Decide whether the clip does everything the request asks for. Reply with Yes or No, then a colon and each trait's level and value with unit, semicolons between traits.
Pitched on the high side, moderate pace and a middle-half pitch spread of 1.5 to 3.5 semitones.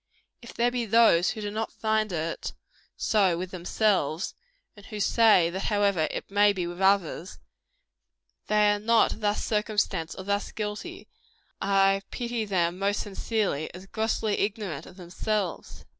Yes: high, 205 Hz; average, 150 wpm; average, 2.8 semitones